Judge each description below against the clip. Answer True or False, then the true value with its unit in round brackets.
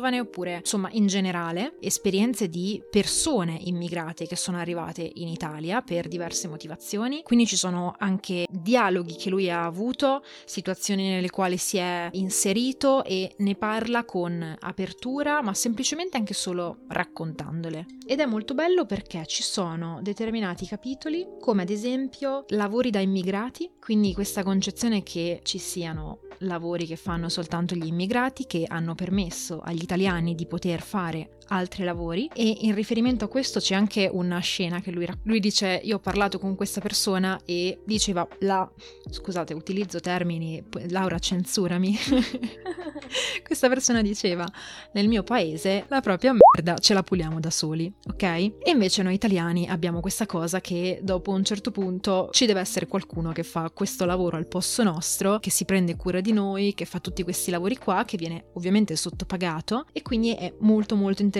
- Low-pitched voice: False (190 Hz)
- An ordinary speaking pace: True (160 wpm)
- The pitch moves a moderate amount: True (3.6 semitones)